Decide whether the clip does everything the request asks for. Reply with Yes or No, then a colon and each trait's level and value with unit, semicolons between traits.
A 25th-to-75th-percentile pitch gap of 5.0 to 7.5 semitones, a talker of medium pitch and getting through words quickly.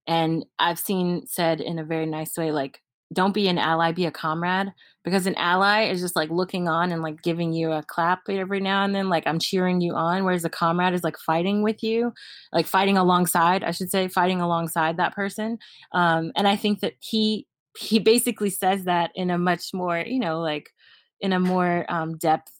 No: average, 2.9 semitones; medium, 180 Hz; fast, 210 wpm